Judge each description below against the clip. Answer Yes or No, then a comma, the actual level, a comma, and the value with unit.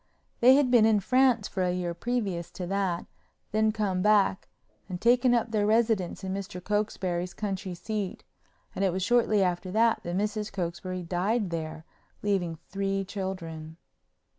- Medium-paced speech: Yes, average, 155 wpm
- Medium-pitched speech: No, high, 195 Hz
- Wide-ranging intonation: No, average, 3.3 semitones